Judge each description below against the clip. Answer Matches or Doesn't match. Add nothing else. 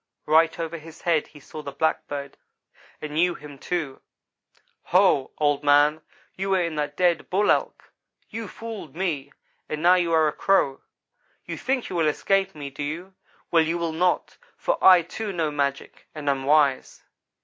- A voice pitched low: Doesn't match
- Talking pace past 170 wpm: Matches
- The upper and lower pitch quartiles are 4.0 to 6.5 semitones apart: Doesn't match